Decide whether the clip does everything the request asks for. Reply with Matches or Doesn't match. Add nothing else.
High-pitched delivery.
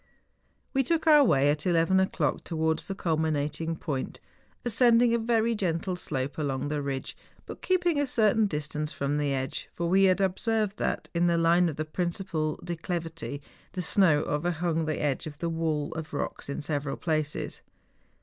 Doesn't match